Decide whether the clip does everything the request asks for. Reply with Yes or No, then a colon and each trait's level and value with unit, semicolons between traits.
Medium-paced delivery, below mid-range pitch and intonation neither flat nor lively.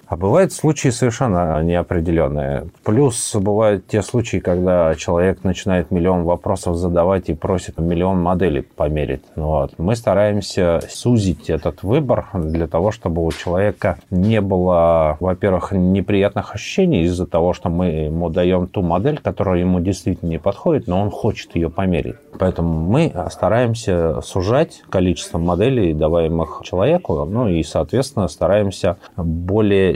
Yes: average, 135 wpm; very low, 90 Hz; average, 3.4 semitones